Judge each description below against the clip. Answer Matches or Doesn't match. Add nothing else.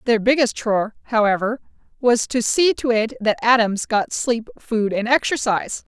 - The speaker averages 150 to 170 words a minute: Matches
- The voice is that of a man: Doesn't match